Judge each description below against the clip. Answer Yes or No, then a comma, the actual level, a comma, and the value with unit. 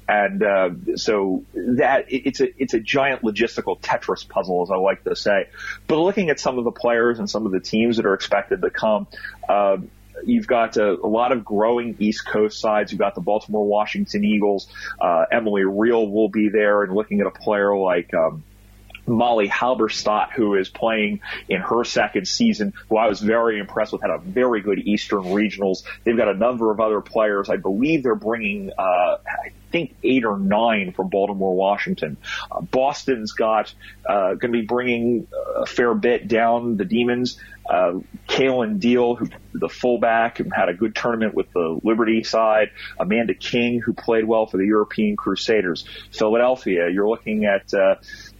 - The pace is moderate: Yes, average, 180 wpm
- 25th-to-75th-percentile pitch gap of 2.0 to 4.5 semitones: Yes, average, 2.8 semitones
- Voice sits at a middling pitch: No, low, 110 Hz